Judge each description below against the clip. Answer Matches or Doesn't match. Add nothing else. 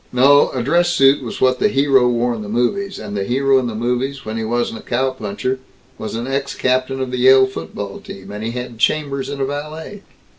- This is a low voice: Matches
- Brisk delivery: Matches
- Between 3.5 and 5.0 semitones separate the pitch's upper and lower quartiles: Doesn't match